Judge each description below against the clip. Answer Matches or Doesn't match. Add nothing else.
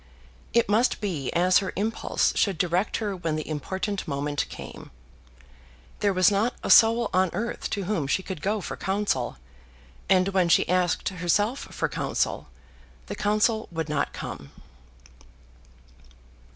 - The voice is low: Doesn't match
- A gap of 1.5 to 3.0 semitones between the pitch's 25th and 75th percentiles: Doesn't match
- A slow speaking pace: Doesn't match